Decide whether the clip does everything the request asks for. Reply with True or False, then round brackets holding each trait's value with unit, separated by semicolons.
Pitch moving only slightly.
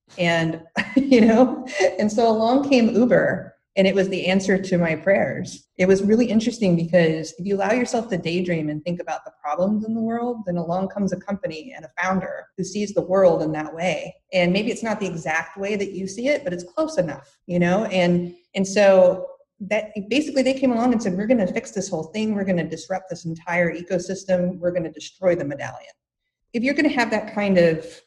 False (4.1 semitones)